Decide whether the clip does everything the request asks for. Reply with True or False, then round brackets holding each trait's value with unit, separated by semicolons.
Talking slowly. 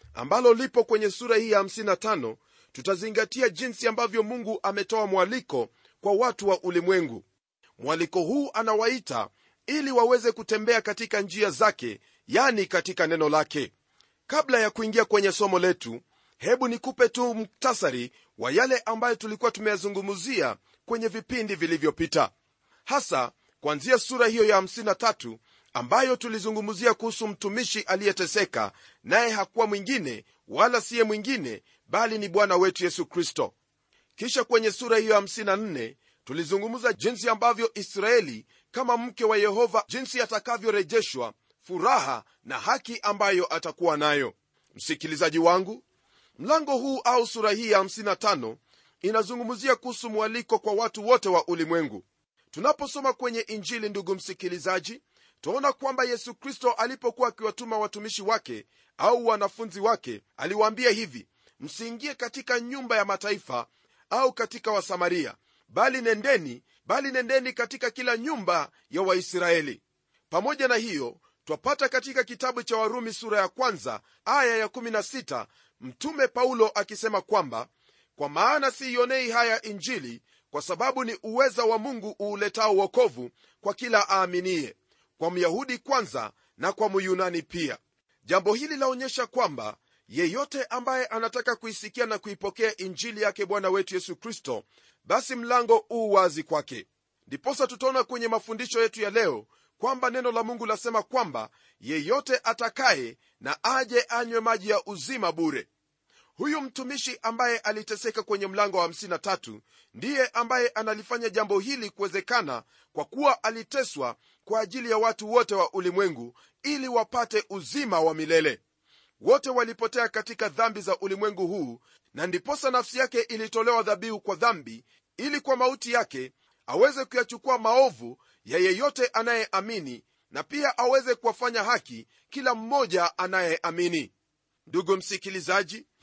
False (125 wpm)